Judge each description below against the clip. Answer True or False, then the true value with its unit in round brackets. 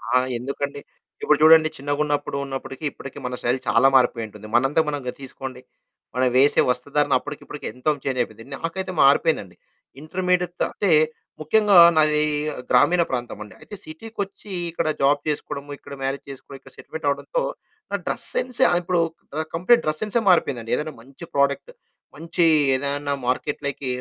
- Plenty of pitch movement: False (3.7 semitones)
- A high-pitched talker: False (145 Hz)